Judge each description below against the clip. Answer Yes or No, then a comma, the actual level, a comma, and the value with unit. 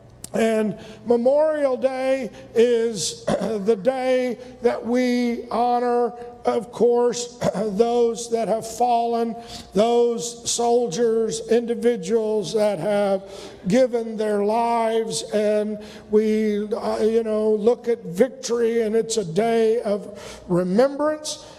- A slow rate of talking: Yes, slow, 100 wpm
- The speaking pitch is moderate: No, high, 230 Hz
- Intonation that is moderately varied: No, narrow, 1.9 semitones